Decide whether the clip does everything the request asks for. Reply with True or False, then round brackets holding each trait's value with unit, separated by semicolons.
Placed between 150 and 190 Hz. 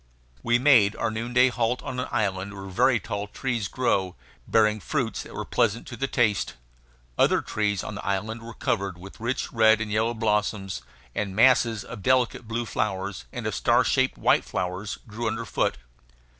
False (110 Hz)